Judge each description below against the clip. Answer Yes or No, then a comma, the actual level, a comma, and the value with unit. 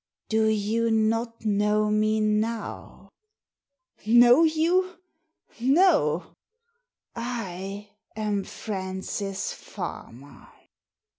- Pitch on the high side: Yes, high, 220 Hz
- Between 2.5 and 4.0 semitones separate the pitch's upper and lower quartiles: Yes, average, 3.1 semitones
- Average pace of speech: No, slow, 85 wpm